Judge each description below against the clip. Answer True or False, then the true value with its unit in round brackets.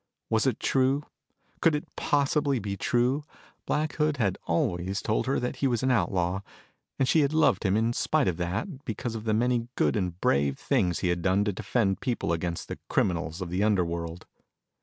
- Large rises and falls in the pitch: True (6.7 semitones)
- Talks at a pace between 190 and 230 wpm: True (195 wpm)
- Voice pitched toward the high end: False (110 Hz)